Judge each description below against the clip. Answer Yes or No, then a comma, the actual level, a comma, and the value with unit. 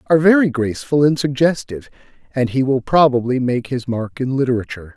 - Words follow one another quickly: No, average, 170 wpm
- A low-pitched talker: Yes, low, 130 Hz